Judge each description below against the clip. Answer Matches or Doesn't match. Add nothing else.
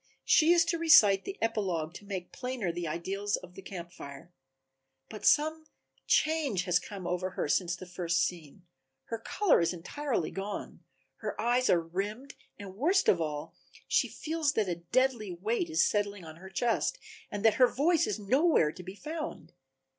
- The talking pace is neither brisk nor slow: Matches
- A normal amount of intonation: Doesn't match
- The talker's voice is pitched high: Matches